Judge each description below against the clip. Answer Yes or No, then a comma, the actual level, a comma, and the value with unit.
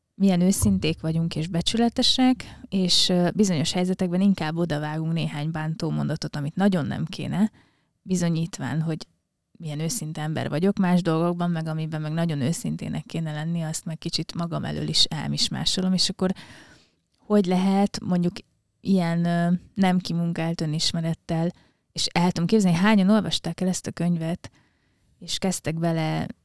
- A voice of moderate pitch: Yes, medium, 170 Hz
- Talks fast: No, average, 140 wpm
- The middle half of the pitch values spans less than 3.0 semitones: Yes, narrow, 2.6 semitones